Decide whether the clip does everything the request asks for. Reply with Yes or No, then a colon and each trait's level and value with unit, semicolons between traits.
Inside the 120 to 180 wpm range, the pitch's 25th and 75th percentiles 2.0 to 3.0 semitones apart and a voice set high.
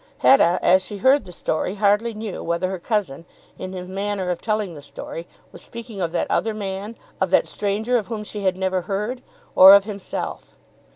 No: average, 195 wpm; narrow, 2.6 semitones; high, 200 Hz